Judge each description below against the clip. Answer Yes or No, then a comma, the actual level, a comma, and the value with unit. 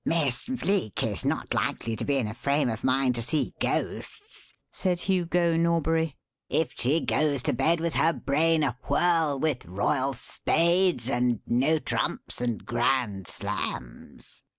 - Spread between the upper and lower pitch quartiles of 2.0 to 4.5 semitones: No, average, 5.2 semitones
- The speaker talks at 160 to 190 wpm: No, average, 150 wpm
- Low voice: No, medium, 145 Hz